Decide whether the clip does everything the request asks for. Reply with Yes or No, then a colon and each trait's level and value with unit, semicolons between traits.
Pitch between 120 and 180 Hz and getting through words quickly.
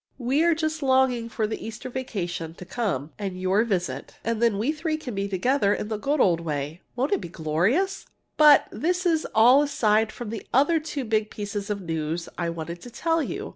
No: high, 220 Hz; fast, 210 wpm